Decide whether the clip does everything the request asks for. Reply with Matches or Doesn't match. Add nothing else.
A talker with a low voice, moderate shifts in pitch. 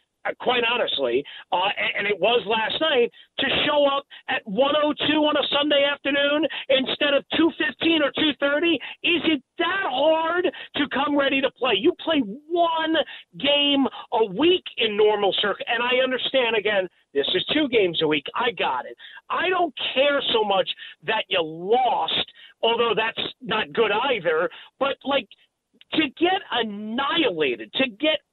Doesn't match